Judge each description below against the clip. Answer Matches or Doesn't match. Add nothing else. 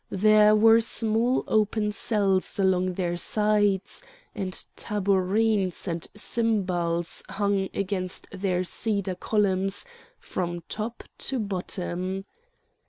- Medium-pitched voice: Doesn't match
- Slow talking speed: Matches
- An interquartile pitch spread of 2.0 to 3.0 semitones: Matches